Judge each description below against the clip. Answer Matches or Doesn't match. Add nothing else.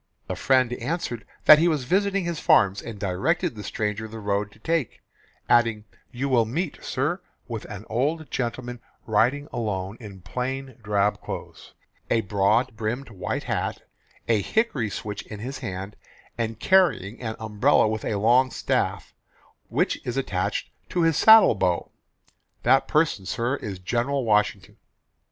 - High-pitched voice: Doesn't match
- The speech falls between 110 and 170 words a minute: Matches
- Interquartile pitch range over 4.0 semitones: Matches